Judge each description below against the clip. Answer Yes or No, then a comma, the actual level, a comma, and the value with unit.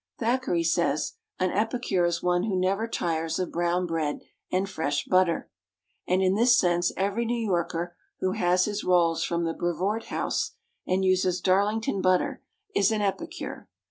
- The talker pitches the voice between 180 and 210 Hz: Yes, medium, 185 Hz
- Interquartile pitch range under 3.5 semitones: Yes, average, 2.9 semitones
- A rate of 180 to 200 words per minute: No, average, 160 wpm